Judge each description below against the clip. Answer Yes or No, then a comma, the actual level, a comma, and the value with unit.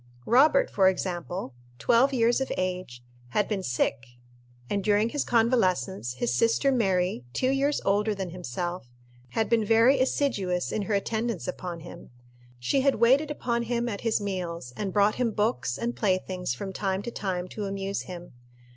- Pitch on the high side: Yes, high, 200 Hz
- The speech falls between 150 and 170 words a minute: Yes, average, 165 wpm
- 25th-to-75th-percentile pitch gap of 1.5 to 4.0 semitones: No, average, 4.6 semitones